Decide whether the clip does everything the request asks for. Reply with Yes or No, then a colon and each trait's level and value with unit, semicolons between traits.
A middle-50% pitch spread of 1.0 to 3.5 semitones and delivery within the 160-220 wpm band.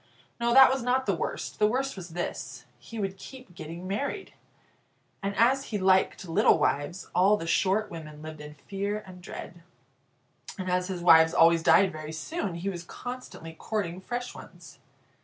No: average, 4.6 semitones; average, 175 wpm